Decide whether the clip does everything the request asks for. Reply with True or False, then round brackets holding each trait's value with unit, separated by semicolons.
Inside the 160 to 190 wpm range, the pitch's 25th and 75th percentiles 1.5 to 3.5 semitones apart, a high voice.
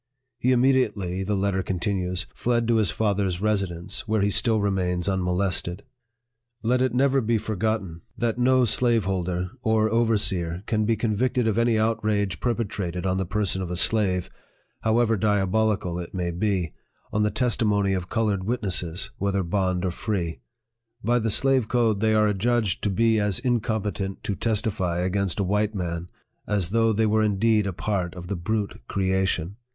False (165 wpm; 3.2 semitones; 105 Hz)